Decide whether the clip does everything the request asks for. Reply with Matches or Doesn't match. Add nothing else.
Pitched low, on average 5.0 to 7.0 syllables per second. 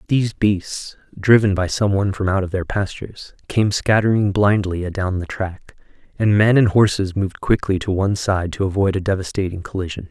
Matches